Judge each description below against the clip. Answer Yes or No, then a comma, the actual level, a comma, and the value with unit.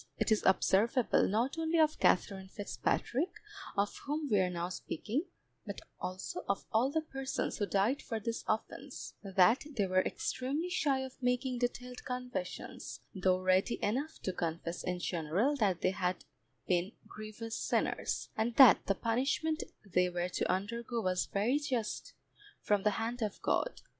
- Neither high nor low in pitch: No, high, 220 Hz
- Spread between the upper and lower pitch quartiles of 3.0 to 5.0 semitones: No, wide, 5.5 semitones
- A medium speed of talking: Yes, average, 160 wpm